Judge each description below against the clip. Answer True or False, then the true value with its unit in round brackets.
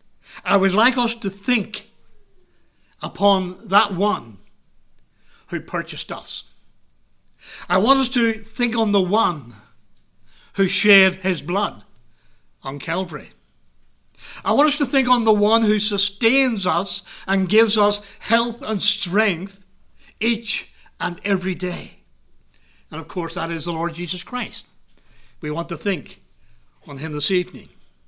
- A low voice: False (195 Hz)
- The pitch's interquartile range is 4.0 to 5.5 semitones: True (4.4 semitones)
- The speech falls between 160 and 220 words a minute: False (135 wpm)